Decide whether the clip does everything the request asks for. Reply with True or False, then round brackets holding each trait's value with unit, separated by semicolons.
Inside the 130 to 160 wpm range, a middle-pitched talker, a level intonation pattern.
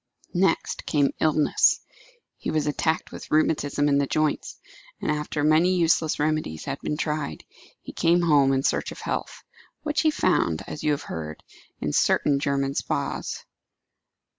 True (155 wpm; 150 Hz; 2.2 semitones)